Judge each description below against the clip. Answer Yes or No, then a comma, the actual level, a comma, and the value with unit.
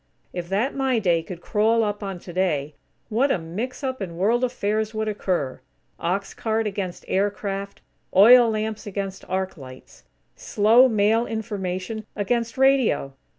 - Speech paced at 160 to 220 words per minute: No, average, 145 wpm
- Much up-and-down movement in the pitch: No, average, 3.4 semitones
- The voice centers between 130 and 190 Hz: No, high, 205 Hz